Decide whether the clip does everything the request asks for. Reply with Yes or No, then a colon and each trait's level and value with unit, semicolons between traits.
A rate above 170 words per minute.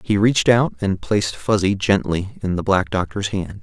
Yes: average, 200 wpm